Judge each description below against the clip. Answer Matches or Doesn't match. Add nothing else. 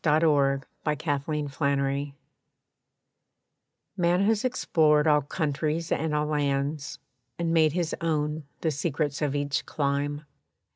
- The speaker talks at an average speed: Doesn't match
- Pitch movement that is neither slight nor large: Doesn't match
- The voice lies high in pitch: Doesn't match